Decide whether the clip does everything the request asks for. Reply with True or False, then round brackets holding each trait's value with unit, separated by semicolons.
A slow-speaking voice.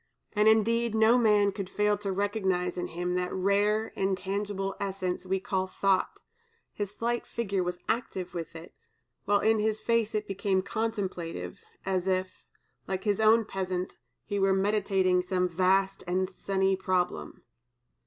False (150 wpm)